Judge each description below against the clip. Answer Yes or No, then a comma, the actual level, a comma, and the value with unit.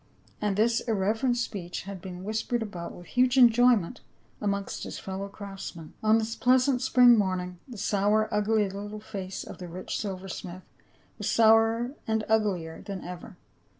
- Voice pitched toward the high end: Yes, high, 210 Hz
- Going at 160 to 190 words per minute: No, average, 150 wpm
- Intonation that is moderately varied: Yes, average, 3.1 semitones